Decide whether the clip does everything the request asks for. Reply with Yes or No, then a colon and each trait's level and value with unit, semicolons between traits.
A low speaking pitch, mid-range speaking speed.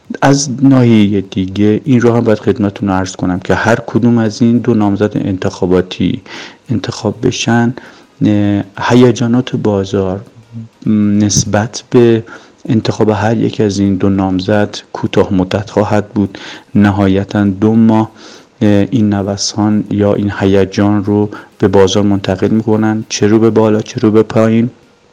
Yes: low, 105 Hz; average, 135 wpm